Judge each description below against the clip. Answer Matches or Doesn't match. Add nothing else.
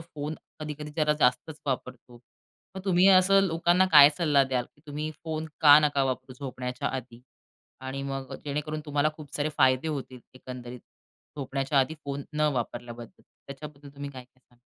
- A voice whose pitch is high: Doesn't match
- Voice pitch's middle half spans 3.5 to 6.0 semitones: Doesn't match